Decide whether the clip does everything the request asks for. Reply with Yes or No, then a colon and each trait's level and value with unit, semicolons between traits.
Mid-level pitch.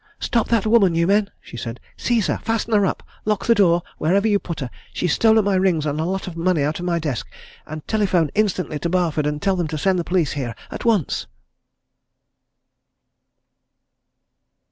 Yes: medium, 180 Hz